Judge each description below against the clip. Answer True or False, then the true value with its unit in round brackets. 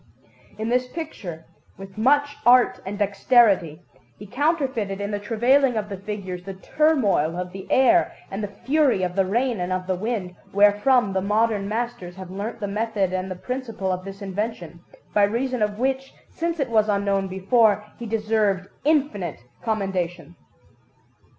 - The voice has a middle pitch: False (205 Hz)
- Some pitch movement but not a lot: True (4.2 semitones)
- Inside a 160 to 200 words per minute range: True (165 wpm)